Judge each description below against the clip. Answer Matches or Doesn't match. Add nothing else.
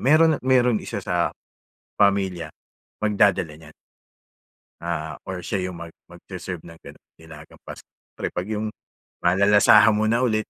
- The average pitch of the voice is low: Matches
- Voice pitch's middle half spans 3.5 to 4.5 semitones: Matches